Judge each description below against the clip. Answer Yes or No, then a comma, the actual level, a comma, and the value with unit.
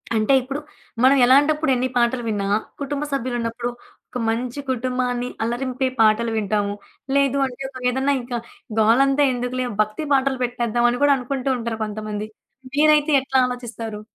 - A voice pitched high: Yes, very high, 250 Hz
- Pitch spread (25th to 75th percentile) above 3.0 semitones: No, average, 2.7 semitones